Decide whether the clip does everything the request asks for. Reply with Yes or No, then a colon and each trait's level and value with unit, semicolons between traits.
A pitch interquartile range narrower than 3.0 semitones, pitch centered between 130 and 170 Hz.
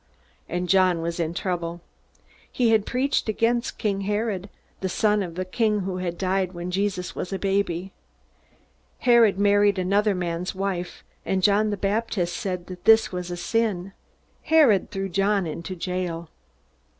No: narrow, 2.6 semitones; high, 190 Hz